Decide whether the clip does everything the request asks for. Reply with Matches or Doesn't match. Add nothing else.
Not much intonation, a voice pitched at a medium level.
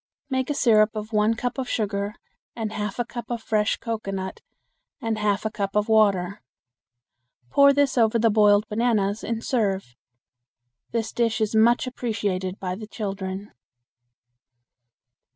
Doesn't match